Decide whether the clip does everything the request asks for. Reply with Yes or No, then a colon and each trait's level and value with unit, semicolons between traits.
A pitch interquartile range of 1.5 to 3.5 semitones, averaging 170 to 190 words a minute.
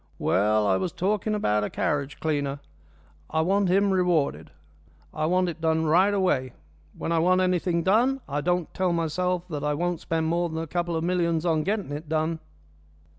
Yes: average, 2.9 semitones; average, 185 wpm